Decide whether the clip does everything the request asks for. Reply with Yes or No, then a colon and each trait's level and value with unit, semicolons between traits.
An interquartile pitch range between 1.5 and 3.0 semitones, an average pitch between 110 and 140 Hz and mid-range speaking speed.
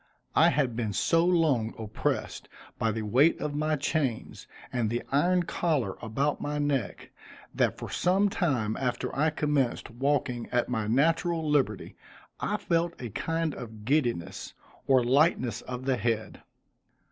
No: average, 5.1 semitones; low, 135 Hz; average, 145 wpm